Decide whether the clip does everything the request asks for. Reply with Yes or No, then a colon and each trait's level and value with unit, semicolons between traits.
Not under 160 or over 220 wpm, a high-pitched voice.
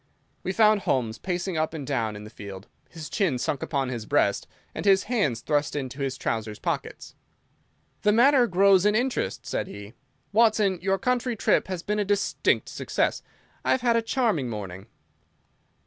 No: average, 175 wpm; medium, 180 Hz